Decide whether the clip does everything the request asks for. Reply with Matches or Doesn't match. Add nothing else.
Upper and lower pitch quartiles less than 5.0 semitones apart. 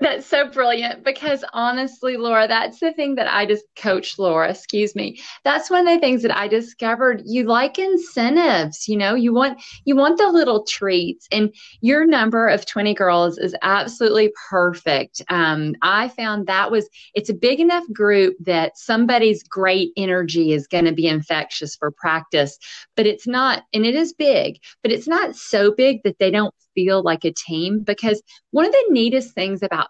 Doesn't match